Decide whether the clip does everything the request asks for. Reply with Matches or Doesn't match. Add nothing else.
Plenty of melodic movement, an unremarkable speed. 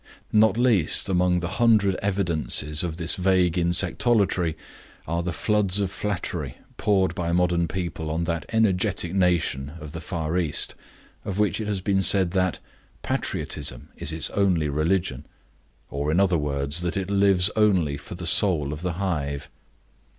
Doesn't match